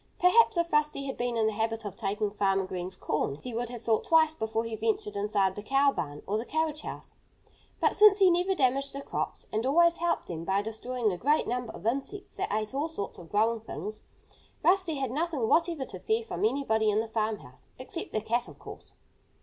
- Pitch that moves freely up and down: Yes, wide, 6.2 semitones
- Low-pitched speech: No, high, 235 Hz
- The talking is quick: Yes, fast, 215 wpm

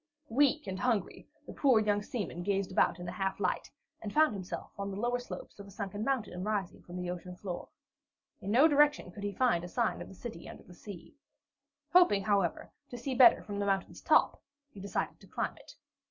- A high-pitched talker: Yes, high, 205 Hz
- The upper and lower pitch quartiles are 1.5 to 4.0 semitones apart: No, average, 4.4 semitones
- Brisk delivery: Yes, fast, 210 wpm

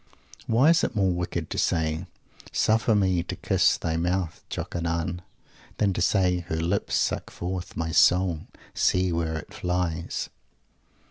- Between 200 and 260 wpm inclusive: No, average, 145 wpm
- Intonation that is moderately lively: No, narrow, 2.2 semitones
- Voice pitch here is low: Yes, very low, 90 Hz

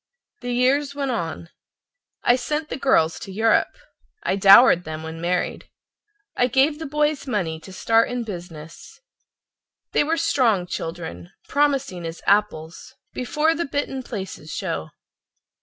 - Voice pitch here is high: Yes, high, 225 Hz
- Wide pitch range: Yes, wide, 8.2 semitones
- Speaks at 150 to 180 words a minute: No, average, 140 wpm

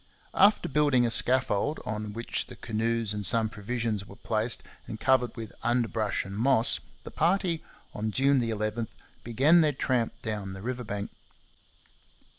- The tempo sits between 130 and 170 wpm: Yes, average, 150 wpm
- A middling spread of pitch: Yes, average, 3.4 semitones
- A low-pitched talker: Yes, low, 115 Hz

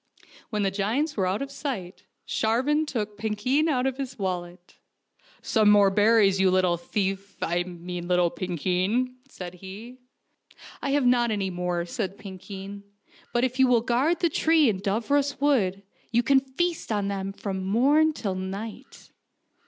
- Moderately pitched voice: No, high, 210 Hz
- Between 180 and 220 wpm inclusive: No, average, 170 wpm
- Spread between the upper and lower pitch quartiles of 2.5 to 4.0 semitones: No, wide, 5.4 semitones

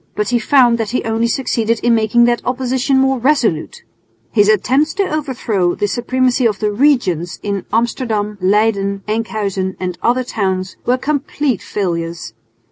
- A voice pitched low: No, high, 225 Hz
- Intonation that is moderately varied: Yes, average, 4.1 semitones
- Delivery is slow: No, average, 150 wpm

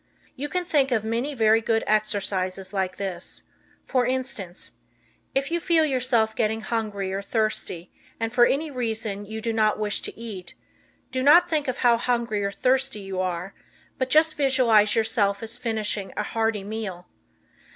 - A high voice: Yes, high, 225 Hz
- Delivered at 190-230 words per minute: No, average, 165 wpm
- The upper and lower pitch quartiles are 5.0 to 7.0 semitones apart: No, average, 4.0 semitones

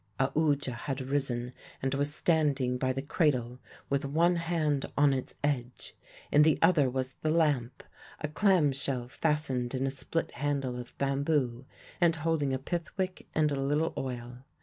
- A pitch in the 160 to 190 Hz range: No, medium, 140 Hz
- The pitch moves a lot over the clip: No, average, 3.0 semitones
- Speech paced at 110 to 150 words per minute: No, average, 165 wpm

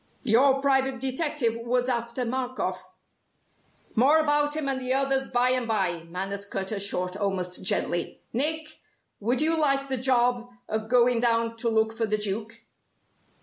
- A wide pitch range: No, average, 3.4 semitones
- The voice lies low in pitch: No, high, 245 Hz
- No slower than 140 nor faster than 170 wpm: Yes, average, 160 wpm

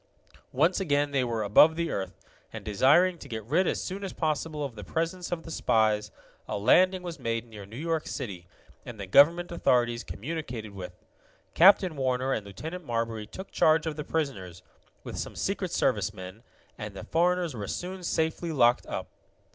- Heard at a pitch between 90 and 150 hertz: Yes, medium, 140 Hz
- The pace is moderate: Yes, average, 180 wpm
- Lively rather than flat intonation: Yes, wide, 7.2 semitones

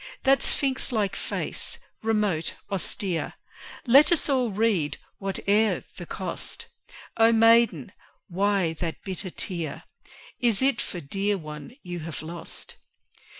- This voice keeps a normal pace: No, slow, 120 wpm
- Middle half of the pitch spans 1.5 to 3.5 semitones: No, average, 4.9 semitones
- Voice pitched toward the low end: No, high, 200 Hz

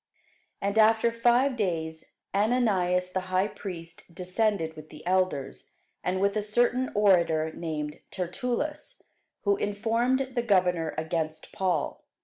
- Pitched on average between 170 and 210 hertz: Yes, high, 190 Hz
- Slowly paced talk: Yes, slow, 125 wpm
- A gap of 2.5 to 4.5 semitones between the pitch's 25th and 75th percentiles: No, average, 5.0 semitones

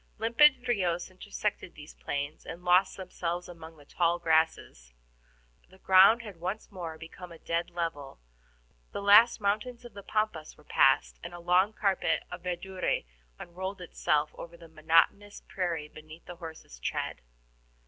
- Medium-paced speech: Yes, average, 150 wpm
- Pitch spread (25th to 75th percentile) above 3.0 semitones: Yes, average, 3.6 semitones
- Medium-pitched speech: Yes, medium, 175 Hz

